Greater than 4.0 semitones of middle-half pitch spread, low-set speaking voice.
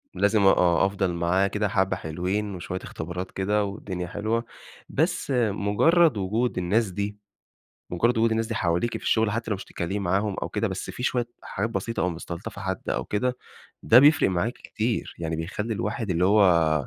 No: average, 3.7 semitones; low, 100 Hz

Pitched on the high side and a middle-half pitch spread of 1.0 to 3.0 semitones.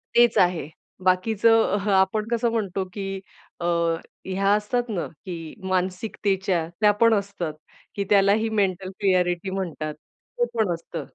Yes: high, 195 Hz; narrow, 2.6 semitones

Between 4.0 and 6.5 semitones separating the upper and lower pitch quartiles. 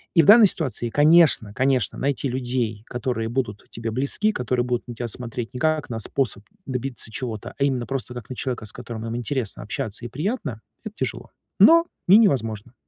No: average, 3.5 semitones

